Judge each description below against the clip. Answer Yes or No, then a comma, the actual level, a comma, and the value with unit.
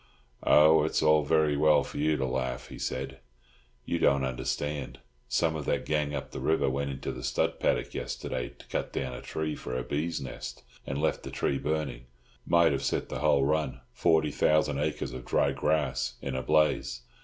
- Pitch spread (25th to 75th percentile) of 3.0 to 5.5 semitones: No, narrow, 2.6 semitones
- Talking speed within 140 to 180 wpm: No, average, 190 wpm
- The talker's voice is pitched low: Yes, very low, 75 Hz